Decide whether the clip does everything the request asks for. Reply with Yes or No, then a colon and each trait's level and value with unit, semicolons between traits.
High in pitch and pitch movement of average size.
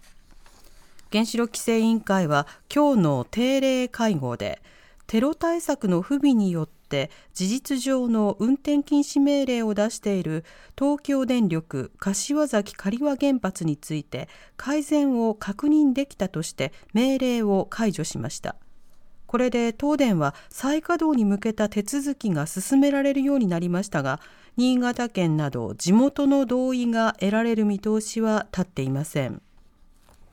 No: high, 225 Hz; wide, 6.8 semitones